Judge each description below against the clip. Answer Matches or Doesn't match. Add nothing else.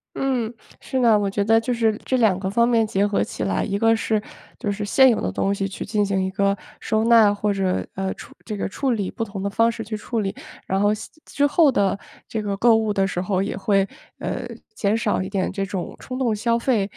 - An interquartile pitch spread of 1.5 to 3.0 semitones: Matches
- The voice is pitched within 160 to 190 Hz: Doesn't match